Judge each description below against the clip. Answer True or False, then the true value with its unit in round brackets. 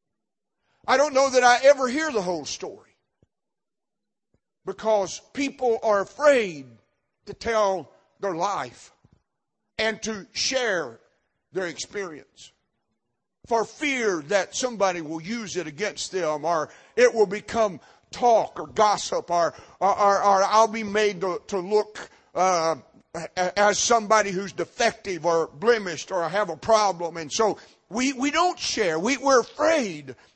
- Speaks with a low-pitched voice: False (210 Hz)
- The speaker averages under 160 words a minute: True (135 wpm)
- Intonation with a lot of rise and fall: False (4.7 semitones)